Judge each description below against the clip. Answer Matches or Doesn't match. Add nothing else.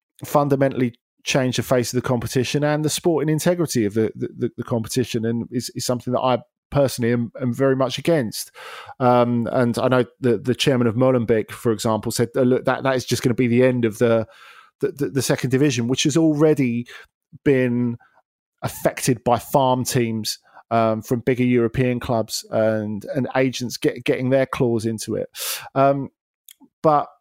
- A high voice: Doesn't match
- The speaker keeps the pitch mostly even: Matches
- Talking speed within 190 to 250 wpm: Doesn't match